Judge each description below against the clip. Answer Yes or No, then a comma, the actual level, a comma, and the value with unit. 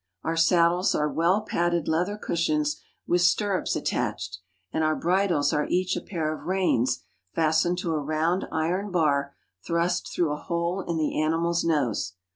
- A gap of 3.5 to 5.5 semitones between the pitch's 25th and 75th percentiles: No, narrow, 2.6 semitones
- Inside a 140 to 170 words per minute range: Yes, average, 160 wpm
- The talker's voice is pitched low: No, medium, 170 Hz